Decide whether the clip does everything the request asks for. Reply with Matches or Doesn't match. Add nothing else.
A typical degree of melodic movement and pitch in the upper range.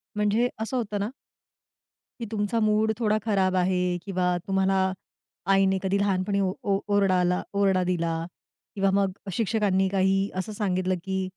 Doesn't match